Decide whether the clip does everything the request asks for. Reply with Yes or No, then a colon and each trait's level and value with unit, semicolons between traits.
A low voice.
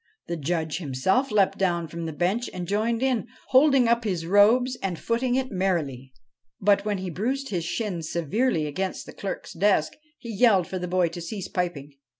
No: high, 190 Hz